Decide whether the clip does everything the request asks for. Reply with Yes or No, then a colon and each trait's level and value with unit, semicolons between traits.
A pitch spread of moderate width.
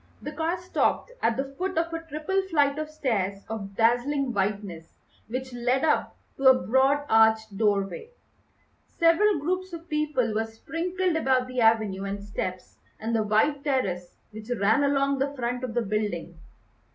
No: wide, 5.9 semitones